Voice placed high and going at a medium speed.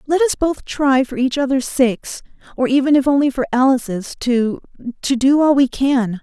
Yes: very high, 265 Hz; average, 185 wpm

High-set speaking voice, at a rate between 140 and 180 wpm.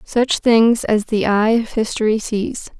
Yes: high, 225 Hz; average, 170 wpm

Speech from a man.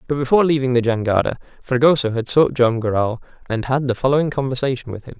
Yes: male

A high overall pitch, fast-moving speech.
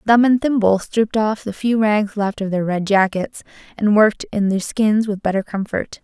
Yes: high, 210 Hz; fast, 210 wpm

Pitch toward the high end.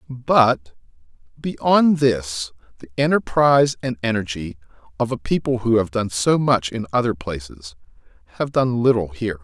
No: low, 115 Hz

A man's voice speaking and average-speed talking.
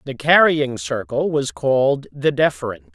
Yes: male; average, 145 wpm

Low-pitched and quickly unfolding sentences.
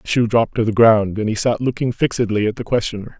Yes: low, 115 Hz; fast, 265 wpm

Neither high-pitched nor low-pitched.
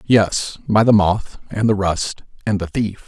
No: low, 100 Hz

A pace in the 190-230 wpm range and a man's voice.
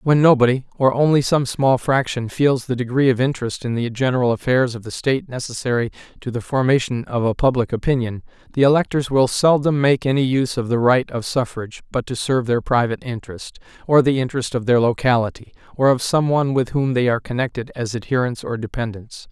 Yes: average, 200 wpm; male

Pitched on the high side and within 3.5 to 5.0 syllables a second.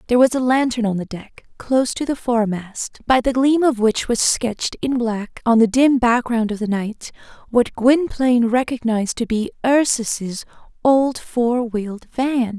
Yes: high, 240 Hz; 4.6 syllables/s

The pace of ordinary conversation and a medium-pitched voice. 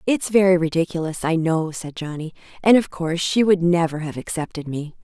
Yes: average, 190 wpm; medium, 170 Hz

